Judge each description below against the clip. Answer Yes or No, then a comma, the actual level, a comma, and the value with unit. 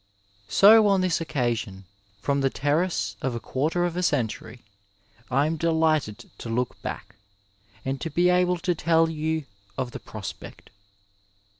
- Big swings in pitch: Yes, wide, 5.7 semitones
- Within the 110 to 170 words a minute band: Yes, average, 150 wpm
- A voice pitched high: No, medium, 150 Hz